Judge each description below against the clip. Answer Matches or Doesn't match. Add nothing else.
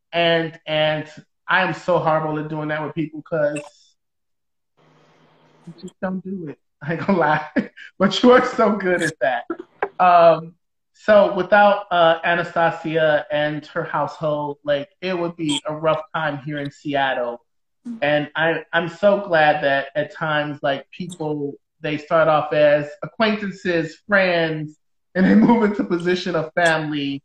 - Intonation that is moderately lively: Matches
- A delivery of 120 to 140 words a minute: Doesn't match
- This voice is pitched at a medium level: Matches